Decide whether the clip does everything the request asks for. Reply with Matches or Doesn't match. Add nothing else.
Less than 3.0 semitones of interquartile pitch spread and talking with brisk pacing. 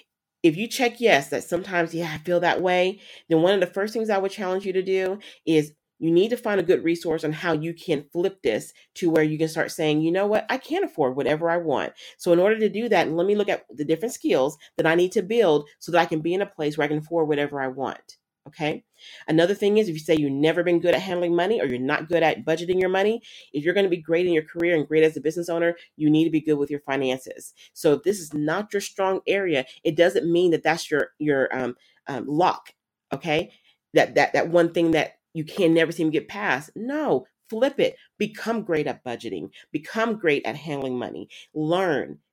Doesn't match